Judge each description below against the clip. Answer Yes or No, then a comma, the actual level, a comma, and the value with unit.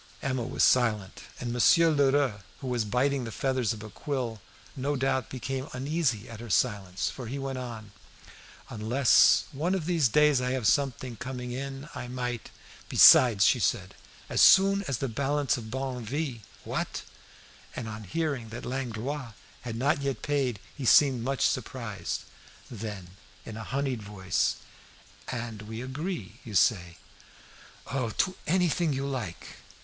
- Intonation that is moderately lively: Yes, average, 3.6 semitones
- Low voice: Yes, low, 125 Hz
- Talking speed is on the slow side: No, average, 155 wpm